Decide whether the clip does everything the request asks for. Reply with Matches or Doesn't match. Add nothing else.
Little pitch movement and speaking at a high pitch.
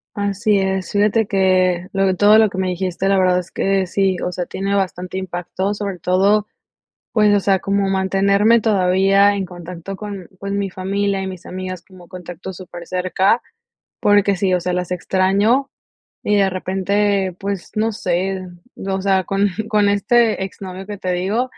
Matches